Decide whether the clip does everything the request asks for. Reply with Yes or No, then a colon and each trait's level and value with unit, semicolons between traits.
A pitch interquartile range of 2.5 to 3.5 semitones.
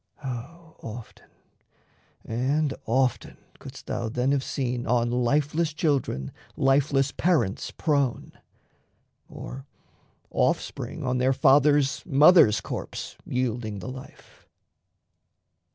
Yes: average, 3.2 semitones